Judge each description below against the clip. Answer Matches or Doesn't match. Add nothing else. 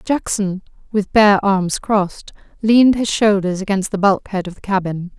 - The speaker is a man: Doesn't match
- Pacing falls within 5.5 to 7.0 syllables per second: Doesn't match